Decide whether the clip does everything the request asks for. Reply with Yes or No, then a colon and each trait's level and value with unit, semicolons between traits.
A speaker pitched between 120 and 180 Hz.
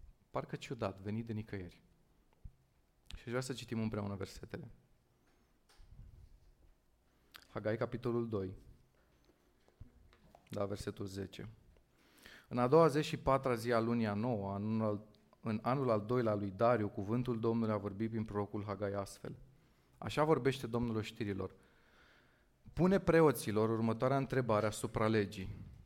No: low, 110 Hz